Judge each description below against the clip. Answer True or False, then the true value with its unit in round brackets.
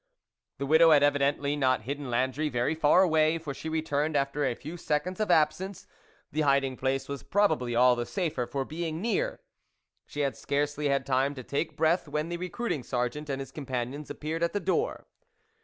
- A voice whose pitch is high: False (145 Hz)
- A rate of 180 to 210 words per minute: True (190 wpm)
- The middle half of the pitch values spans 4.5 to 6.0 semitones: False (2.9 semitones)